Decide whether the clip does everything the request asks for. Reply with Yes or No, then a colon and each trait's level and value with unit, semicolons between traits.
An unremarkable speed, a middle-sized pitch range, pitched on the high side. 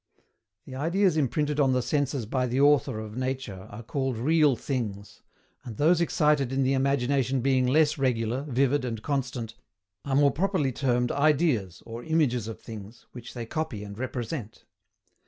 No: average, 160 wpm; average, 3.6 semitones; low, 130 Hz